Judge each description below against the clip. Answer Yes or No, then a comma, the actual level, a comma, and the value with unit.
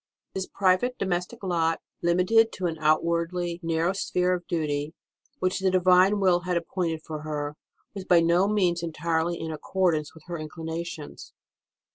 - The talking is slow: No, average, 155 wpm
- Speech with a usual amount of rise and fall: No, narrow, 2.2 semitones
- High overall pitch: No, medium, 170 Hz